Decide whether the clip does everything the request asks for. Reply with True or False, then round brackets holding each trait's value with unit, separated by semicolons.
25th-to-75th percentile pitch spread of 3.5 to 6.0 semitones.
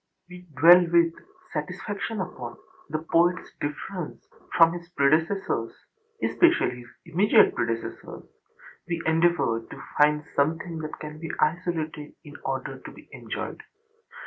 False (2.8 semitones)